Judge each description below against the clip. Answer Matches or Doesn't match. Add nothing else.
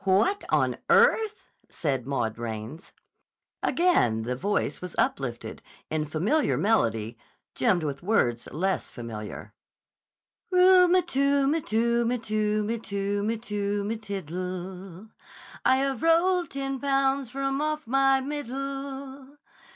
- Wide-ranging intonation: Matches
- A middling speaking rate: Doesn't match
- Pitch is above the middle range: Matches